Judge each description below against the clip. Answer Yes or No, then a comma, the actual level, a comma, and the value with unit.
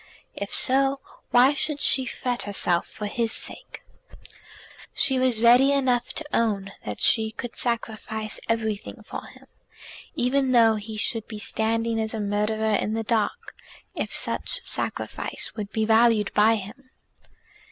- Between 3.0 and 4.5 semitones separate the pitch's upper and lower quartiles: No, narrow, 2.6 semitones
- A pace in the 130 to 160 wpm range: Yes, average, 145 wpm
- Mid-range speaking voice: No, high, 225 Hz